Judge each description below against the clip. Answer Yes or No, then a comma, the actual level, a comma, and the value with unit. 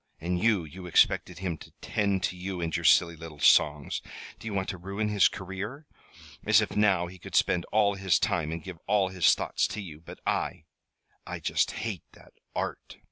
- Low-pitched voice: Yes, very low, 95 Hz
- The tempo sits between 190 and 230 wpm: Yes, average, 200 wpm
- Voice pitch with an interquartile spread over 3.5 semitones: No, average, 3.0 semitones